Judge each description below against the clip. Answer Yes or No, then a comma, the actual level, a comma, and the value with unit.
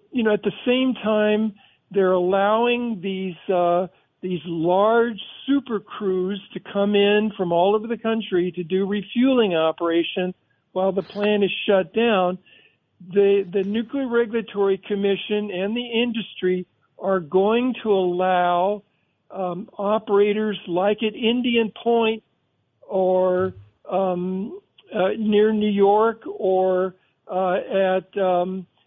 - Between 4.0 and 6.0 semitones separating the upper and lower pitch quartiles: No, average, 2.7 semitones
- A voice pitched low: No, high, 200 Hz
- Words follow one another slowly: Yes, slow, 125 wpm